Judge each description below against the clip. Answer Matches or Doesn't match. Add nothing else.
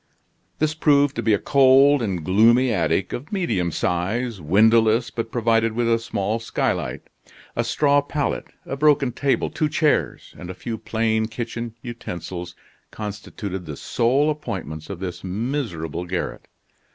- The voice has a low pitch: Matches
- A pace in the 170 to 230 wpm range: Doesn't match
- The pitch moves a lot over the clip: Matches